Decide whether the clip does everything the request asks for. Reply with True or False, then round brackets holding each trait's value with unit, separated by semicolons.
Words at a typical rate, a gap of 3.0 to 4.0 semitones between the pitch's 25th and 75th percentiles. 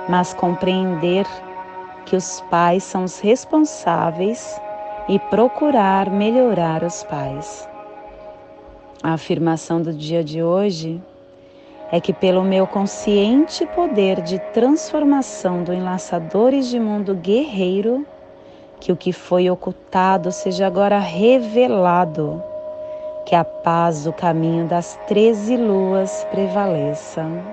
False (105 wpm; 3.4 semitones)